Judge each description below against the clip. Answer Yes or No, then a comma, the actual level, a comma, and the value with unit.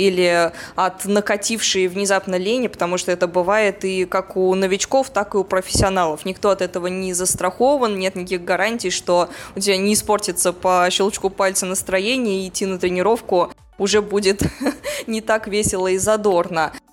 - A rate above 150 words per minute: Yes, fast, 160 wpm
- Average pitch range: No, narrow, 2.1 semitones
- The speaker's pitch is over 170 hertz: Yes, high, 190 Hz